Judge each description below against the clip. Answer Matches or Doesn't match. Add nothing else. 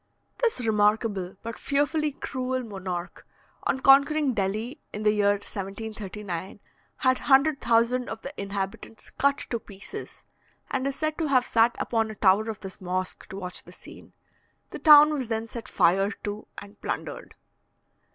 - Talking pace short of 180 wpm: Matches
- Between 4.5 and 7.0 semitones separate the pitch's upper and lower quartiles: Matches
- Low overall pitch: Doesn't match